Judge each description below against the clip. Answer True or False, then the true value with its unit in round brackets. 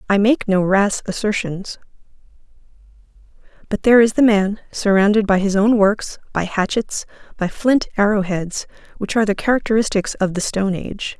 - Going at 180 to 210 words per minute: False (155 wpm)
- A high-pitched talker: True (205 Hz)